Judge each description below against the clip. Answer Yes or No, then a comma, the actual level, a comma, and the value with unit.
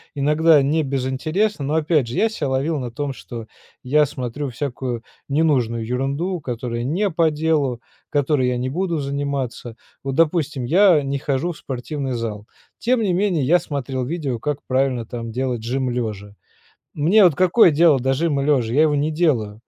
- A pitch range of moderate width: Yes, average, 4.0 semitones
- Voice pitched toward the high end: No, medium, 140 Hz